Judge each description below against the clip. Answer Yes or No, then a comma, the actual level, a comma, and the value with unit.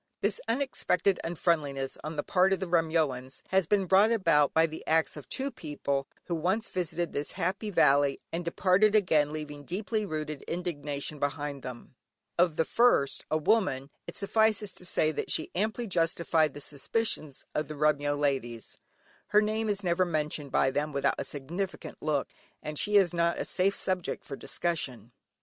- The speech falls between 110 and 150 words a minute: No, average, 170 wpm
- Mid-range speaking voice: Yes, medium, 165 Hz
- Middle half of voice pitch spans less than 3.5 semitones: No, average, 4.6 semitones